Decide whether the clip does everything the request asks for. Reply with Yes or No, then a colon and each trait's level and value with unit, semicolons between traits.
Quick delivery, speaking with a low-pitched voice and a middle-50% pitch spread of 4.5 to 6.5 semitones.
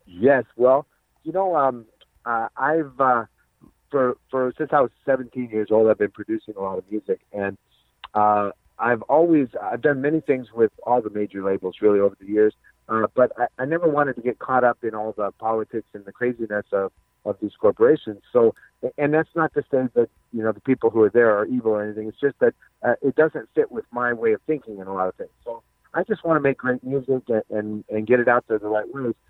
Yes: fast, 235 wpm; low, 120 Hz; average, 4.8 semitones